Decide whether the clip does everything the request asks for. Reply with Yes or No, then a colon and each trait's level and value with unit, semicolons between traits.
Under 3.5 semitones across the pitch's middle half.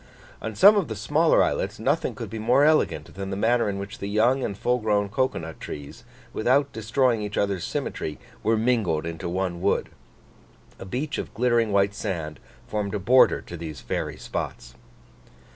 No: average, 4.3 semitones